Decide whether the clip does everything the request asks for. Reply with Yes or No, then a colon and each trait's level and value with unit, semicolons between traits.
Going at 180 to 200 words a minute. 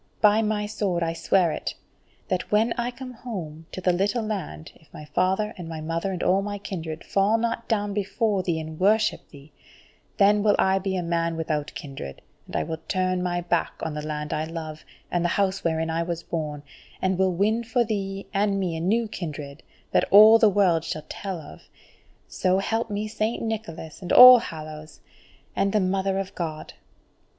Yes: average, 195 wpm